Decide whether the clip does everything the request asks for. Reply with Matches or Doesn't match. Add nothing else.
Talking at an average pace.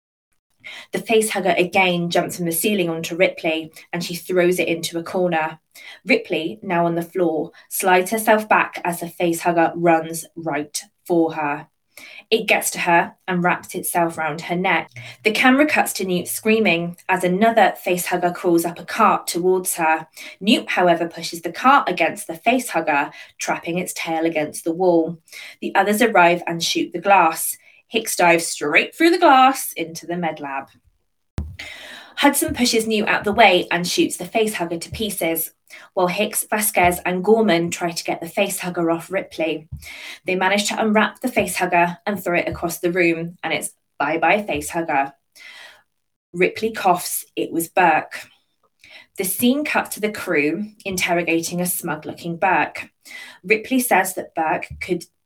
Matches